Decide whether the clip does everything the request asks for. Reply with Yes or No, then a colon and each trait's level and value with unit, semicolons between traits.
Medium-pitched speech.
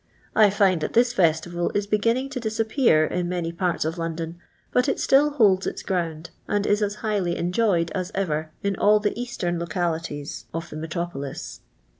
Yes: medium, 180 Hz